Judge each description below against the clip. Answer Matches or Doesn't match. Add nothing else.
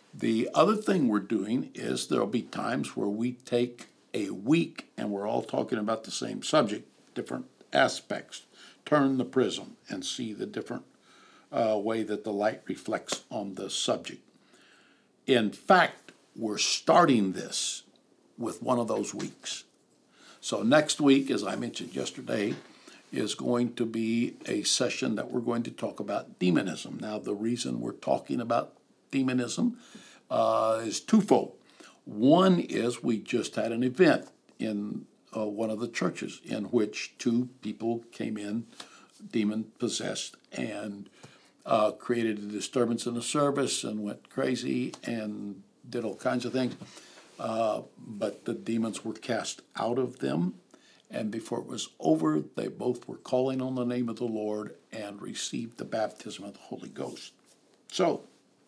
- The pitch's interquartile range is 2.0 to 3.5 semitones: Matches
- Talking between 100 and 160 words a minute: Matches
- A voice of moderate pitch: Doesn't match